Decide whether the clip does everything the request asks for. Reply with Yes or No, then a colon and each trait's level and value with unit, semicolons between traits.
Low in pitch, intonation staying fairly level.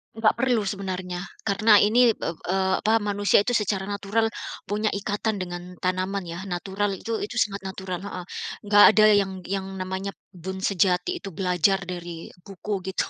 No: high, 195 Hz; narrow, 2.0 semitones